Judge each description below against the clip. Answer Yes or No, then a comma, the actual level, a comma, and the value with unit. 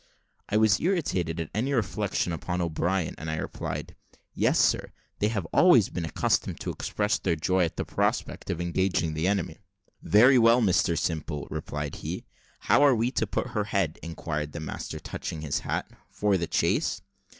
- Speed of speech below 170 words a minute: No, average, 175 wpm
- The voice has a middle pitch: No, very low, 90 Hz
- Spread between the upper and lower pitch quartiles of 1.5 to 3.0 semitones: No, average, 4.6 semitones